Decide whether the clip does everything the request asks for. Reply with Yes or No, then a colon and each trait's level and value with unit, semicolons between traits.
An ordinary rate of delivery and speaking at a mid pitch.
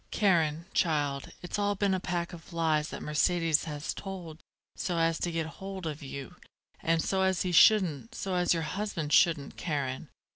Yes: average, 180 wpm; medium, 165 Hz